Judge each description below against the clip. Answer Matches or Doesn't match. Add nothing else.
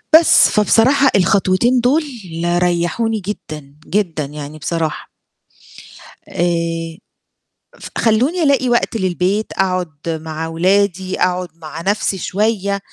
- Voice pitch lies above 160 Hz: Matches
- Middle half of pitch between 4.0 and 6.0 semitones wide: Matches